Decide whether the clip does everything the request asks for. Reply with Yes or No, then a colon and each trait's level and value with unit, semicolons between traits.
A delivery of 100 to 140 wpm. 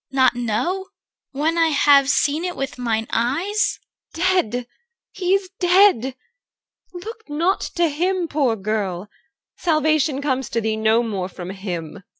No: average, 150 wpm